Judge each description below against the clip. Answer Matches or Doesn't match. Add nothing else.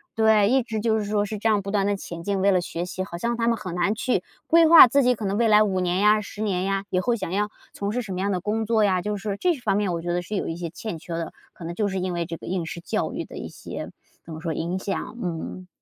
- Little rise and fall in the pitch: Doesn't match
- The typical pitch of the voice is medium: Doesn't match